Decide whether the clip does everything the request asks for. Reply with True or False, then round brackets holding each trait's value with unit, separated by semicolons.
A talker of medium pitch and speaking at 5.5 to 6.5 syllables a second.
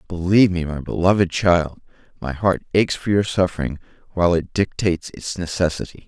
False (90 Hz; 5.7 syllables/s)